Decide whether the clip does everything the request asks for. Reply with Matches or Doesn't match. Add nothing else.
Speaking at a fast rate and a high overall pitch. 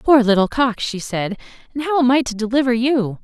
Matches